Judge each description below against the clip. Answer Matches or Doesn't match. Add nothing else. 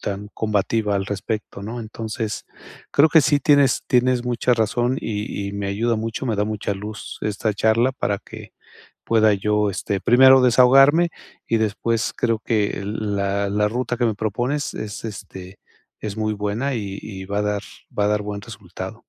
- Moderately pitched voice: Doesn't match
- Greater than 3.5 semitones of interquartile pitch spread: Doesn't match